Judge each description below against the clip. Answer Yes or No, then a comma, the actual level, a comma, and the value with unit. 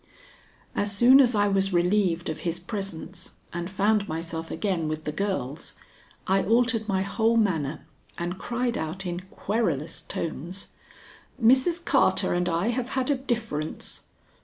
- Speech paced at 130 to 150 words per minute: Yes, average, 145 wpm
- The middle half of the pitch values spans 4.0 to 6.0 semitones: Yes, average, 5.2 semitones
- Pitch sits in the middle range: No, high, 195 Hz